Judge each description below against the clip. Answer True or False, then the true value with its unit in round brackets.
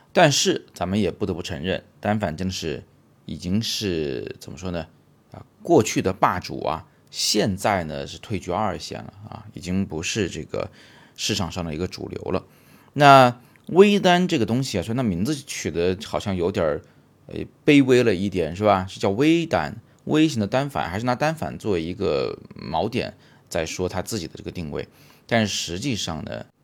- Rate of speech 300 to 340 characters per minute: False (265 characters per minute)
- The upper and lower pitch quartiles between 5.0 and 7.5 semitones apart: True (5.3 semitones)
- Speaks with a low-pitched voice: True (105 Hz)